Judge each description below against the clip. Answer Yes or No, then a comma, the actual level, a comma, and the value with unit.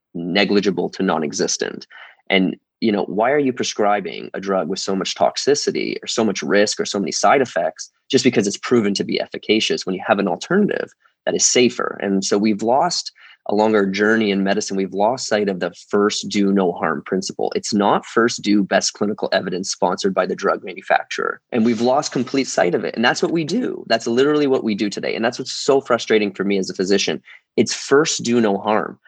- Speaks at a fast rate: Yes, fast, 215 wpm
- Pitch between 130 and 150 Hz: No, low, 105 Hz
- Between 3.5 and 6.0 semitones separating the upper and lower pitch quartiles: Yes, average, 4.0 semitones